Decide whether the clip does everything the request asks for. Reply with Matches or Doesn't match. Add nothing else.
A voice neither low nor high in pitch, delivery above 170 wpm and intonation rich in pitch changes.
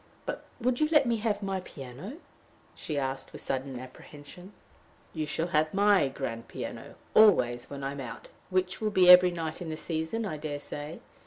Matches